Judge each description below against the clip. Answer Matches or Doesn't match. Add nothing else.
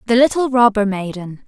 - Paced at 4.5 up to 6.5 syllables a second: Matches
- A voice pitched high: Matches